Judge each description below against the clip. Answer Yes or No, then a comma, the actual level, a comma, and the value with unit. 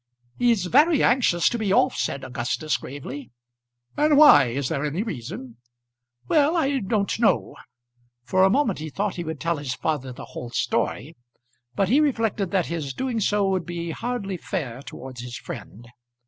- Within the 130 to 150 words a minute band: No, average, 170 wpm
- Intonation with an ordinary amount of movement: No, wide, 8.7 semitones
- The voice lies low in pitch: No, medium, 175 Hz